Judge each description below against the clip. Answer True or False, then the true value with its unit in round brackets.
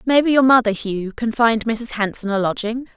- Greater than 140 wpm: True (205 wpm)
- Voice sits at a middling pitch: False (225 Hz)